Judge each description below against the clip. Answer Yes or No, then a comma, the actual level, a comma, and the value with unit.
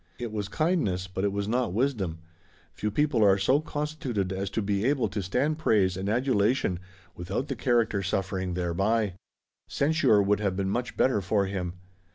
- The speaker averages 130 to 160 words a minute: No, average, 175 wpm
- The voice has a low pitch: Yes, low, 105 Hz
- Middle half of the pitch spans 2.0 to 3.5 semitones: No, average, 4.7 semitones